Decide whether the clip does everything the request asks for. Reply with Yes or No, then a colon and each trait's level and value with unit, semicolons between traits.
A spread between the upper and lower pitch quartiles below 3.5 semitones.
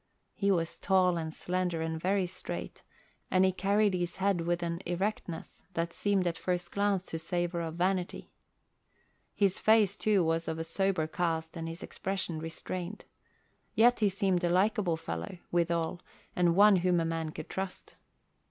Yes: average, 2.7 semitones